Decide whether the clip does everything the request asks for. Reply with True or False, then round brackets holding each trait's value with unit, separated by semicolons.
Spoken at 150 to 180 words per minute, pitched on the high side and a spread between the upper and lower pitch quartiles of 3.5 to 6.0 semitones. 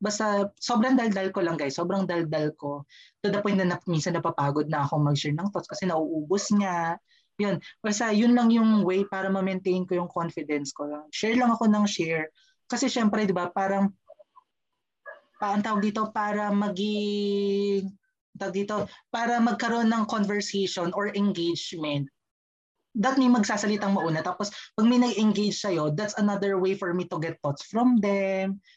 True (165 wpm; 200 Hz; 3.9 semitones)